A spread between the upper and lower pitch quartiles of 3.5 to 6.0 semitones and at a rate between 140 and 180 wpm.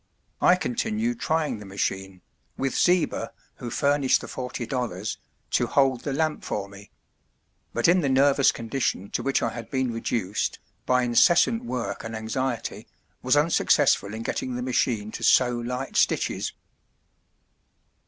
Yes: average, 3.8 semitones; average, 145 wpm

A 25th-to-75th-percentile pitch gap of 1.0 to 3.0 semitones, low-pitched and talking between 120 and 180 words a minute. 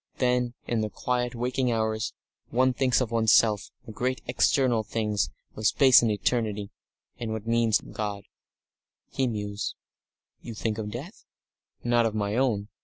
Yes: narrow, 2.5 semitones; low, 115 Hz; average, 170 wpm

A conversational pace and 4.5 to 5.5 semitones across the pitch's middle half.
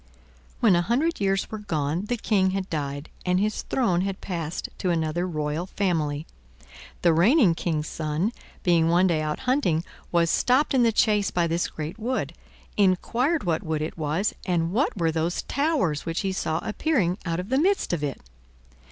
Yes: average, 180 wpm; average, 4.8 semitones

